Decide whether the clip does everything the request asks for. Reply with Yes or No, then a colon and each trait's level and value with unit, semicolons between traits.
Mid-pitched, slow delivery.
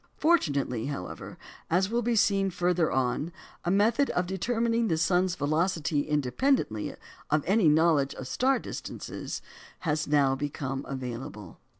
Yes: medium, 160 Hz; slow, 130 wpm